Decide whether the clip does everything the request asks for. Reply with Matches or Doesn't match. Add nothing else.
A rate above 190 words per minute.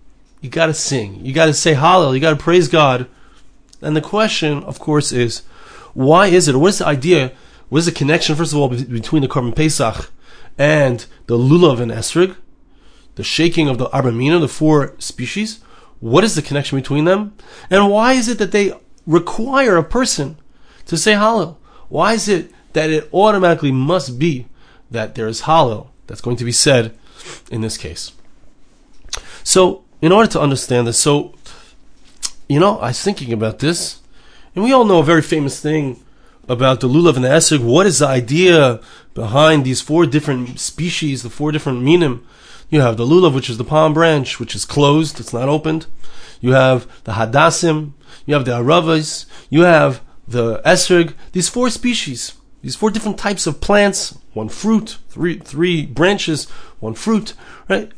Doesn't match